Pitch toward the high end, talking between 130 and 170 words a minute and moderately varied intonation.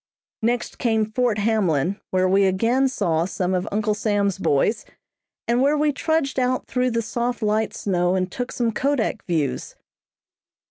Yes: high, 215 Hz; average, 155 wpm; average, 4.7 semitones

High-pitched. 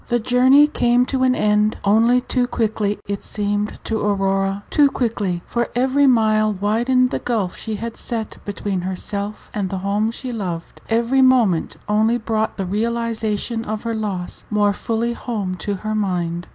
Yes: high, 215 Hz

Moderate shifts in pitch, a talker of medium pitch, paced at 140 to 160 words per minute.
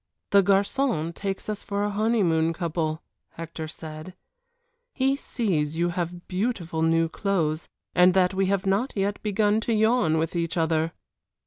Yes: average, 4.0 semitones; medium, 180 Hz; average, 150 wpm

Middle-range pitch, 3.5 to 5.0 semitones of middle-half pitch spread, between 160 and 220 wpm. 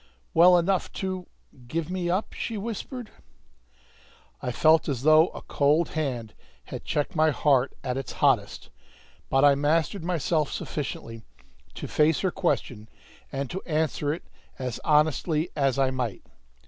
No: medium, 155 Hz; average, 4.2 semitones; average, 145 wpm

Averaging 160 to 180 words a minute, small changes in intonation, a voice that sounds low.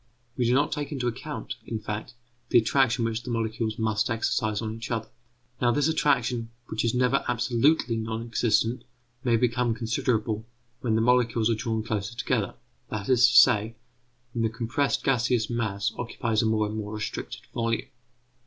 Yes: average, 170 wpm; narrow, 1.9 semitones; low, 115 Hz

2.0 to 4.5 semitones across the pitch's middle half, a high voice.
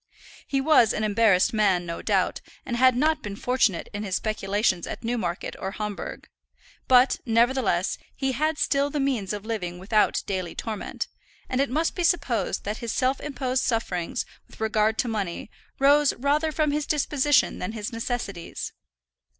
No: average, 5.0 semitones; high, 230 Hz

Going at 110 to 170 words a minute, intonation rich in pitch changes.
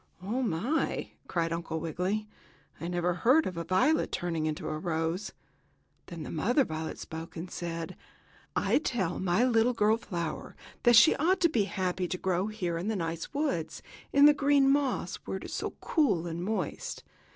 No: average, 180 wpm; wide, 6.2 semitones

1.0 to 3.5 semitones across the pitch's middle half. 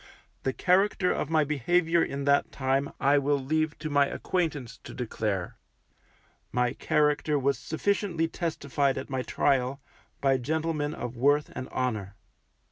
Yes: average, 3.1 semitones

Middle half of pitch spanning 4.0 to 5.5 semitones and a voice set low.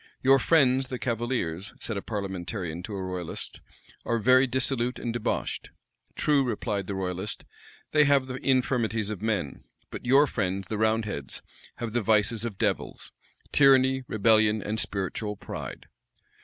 Yes: average, 4.5 semitones; low, 110 Hz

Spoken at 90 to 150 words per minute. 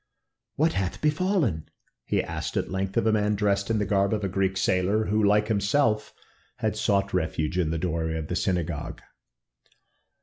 No: average, 175 wpm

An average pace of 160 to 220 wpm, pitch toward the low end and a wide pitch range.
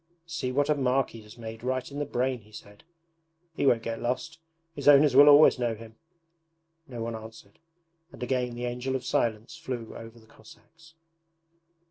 No: average, 180 wpm; low, 125 Hz; average, 3.7 semitones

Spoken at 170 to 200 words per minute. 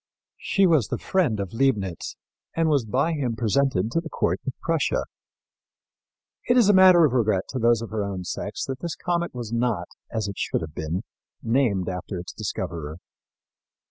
Yes: average, 180 wpm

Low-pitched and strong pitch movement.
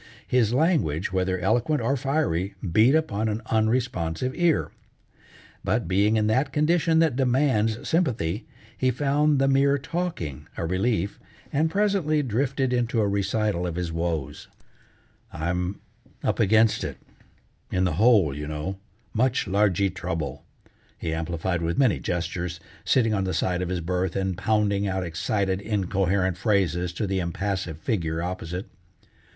Yes: low, 100 Hz; wide, 6.2 semitones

